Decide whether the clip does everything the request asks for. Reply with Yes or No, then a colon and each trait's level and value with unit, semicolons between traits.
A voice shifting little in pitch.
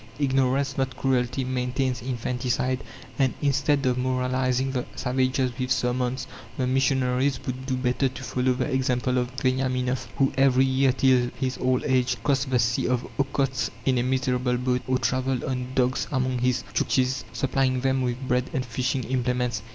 Yes: narrow, 0.9 semitones